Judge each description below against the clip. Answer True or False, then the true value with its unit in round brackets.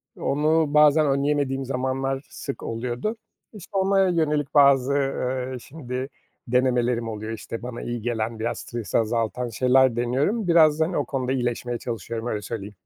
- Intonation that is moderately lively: True (3.6 semitones)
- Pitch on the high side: False (130 Hz)